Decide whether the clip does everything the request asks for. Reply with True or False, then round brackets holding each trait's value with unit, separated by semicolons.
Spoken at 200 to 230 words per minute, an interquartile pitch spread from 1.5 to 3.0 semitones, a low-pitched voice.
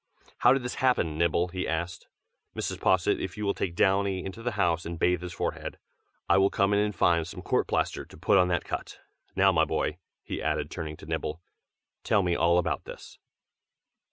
True (205 wpm; 2.7 semitones; 90 Hz)